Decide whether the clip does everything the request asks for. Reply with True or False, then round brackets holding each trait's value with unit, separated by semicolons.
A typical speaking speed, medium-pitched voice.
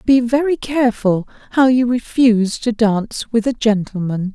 False (150 wpm; 230 Hz)